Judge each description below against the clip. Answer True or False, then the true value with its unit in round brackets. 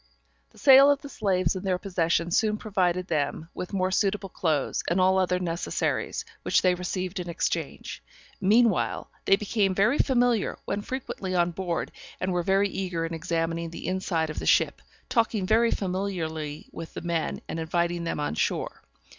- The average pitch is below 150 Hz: False (185 Hz)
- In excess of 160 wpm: True (170 wpm)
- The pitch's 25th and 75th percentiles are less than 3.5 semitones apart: True (3.0 semitones)